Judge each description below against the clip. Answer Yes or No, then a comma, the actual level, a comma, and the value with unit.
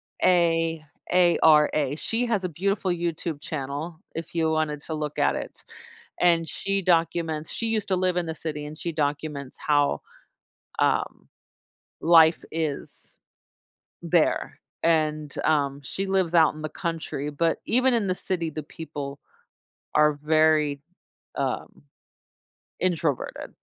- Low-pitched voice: No, medium, 160 Hz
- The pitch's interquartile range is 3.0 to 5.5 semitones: No, narrow, 2.5 semitones